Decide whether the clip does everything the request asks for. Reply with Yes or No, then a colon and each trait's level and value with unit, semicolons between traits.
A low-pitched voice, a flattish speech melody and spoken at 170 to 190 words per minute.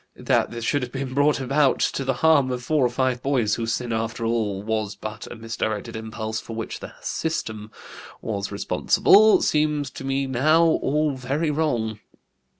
No: low, 125 Hz; average, 4.3 semitones; average, 175 wpm